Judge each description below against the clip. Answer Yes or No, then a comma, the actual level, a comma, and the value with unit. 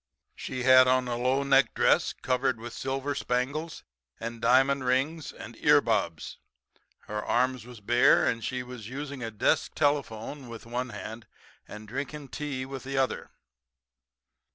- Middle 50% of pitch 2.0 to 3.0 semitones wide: Yes, narrow, 2.5 semitones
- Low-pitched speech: Yes, low, 130 Hz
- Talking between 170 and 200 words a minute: No, average, 155 wpm